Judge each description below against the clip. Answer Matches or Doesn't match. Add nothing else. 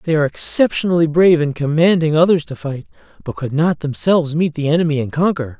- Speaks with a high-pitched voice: Doesn't match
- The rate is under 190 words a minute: Doesn't match